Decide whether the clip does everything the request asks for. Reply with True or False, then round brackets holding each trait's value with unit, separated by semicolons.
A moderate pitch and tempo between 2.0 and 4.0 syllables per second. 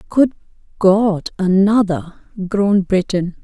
False (195 Hz; 3.8 syllables/s)